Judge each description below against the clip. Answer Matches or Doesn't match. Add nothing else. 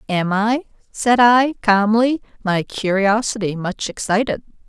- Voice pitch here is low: Doesn't match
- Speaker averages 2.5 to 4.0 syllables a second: Matches